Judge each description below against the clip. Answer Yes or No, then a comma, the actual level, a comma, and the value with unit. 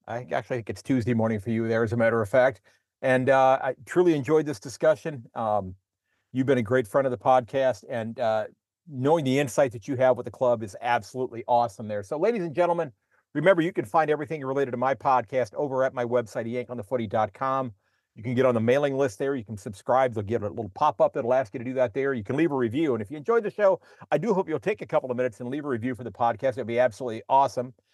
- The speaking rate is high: Yes, fast, 250 wpm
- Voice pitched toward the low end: Yes, low, 130 Hz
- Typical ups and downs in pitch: Yes, average, 3.0 semitones